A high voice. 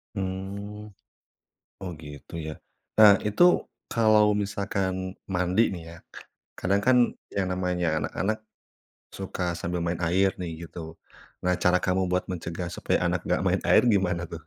No: very low, 95 Hz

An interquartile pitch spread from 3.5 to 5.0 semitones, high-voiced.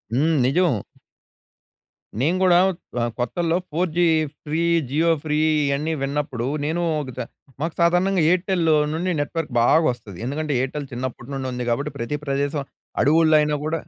No: average, 3.8 semitones; medium, 150 Hz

